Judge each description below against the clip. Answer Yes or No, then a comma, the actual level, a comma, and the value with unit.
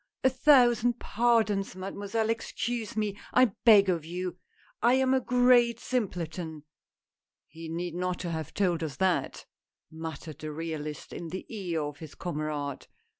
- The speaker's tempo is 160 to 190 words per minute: No, average, 150 wpm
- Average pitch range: No, wide, 6.2 semitones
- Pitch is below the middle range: No, medium, 185 Hz